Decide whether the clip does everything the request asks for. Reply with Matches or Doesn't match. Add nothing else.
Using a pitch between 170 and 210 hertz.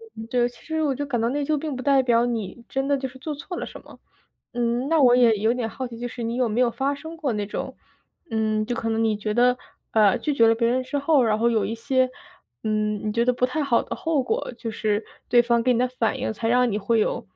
Doesn't match